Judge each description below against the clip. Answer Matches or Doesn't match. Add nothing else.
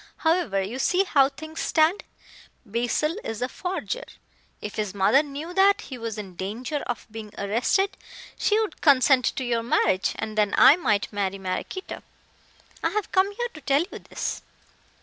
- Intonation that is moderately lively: Doesn't match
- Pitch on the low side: Doesn't match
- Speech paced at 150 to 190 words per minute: Matches